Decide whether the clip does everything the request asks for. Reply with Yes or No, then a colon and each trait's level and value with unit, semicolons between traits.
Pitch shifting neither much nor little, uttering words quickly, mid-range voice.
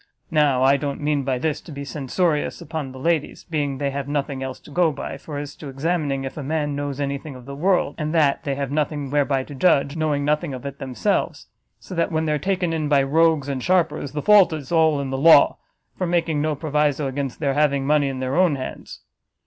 No: narrow, 2.3 semitones; fast, 235 wpm; medium, 145 Hz